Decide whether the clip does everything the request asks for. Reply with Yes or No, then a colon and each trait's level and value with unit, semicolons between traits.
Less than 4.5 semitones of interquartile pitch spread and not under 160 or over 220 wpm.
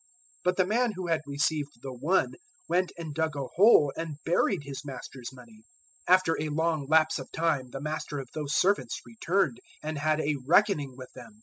Yes: average, 3.7 semitones; average, 200 wpm